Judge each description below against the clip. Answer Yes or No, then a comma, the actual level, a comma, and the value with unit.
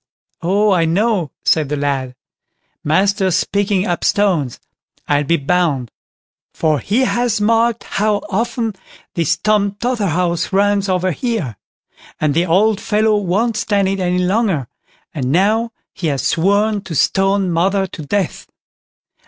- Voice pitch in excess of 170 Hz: Yes, high, 190 Hz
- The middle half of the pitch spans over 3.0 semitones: Yes, average, 4.1 semitones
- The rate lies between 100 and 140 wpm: Yes, slow, 135 wpm